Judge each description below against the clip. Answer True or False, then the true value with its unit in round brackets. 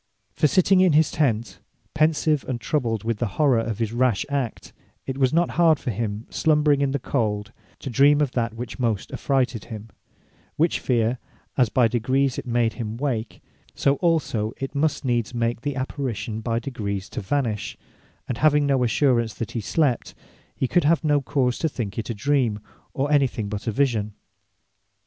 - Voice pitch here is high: False (125 Hz)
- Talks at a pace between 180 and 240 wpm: True (185 wpm)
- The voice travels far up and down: False (4.1 semitones)